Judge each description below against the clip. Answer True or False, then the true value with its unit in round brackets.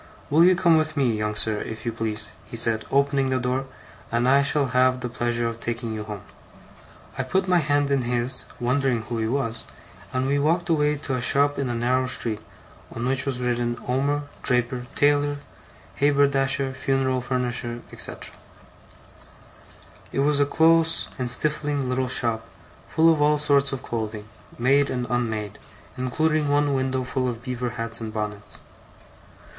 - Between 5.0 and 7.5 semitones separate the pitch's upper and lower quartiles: False (3.2 semitones)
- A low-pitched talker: True (130 Hz)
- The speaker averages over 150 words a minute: True (170 wpm)